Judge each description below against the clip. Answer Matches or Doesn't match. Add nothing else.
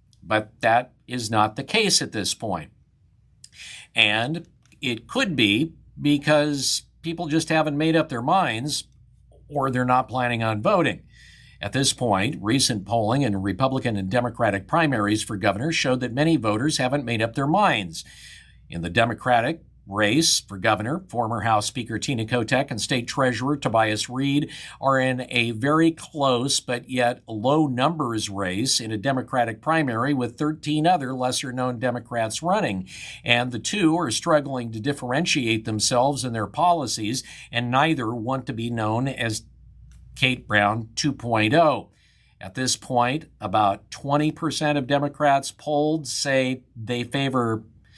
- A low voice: Matches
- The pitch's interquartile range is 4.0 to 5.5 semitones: Matches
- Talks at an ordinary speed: Matches